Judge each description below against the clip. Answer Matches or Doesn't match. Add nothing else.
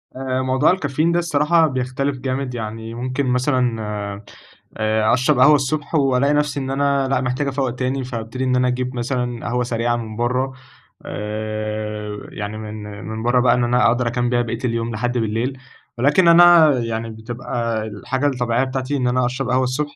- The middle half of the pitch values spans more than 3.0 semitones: Doesn't match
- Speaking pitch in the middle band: Doesn't match